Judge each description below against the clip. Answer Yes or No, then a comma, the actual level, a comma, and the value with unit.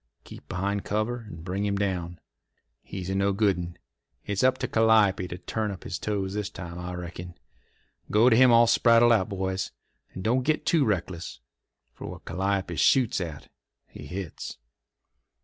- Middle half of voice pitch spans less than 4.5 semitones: Yes, average, 3.7 semitones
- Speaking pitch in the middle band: No, low, 100 Hz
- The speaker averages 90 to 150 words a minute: No, average, 165 wpm